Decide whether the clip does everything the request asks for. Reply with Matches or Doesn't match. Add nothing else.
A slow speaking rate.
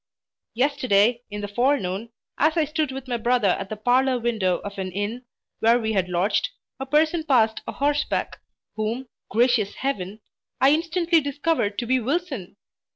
Doesn't match